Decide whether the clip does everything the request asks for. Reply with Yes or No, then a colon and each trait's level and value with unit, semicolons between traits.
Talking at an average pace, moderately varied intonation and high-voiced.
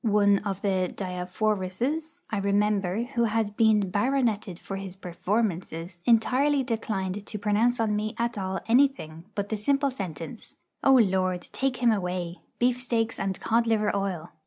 Yes: average, 155 wpm; average, 3.7 semitones; high, 210 Hz